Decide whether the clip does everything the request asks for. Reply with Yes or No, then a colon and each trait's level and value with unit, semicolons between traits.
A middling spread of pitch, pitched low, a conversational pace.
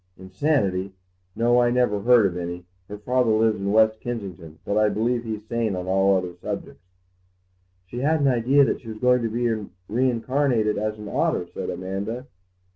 Yes: average, 3.8 semitones; low, 110 Hz; average, 180 wpm